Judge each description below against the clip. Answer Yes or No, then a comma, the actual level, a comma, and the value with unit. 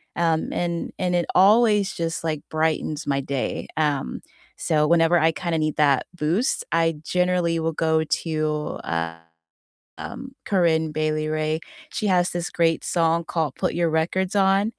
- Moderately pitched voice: Yes, medium, 165 Hz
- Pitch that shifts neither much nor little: No, narrow, 2.3 semitones